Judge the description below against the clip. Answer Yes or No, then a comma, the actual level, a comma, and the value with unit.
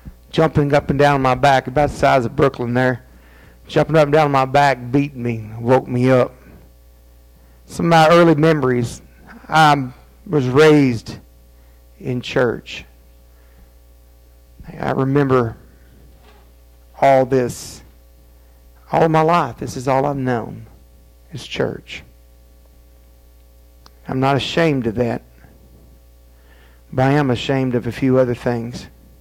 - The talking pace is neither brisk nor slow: No, slow, 125 wpm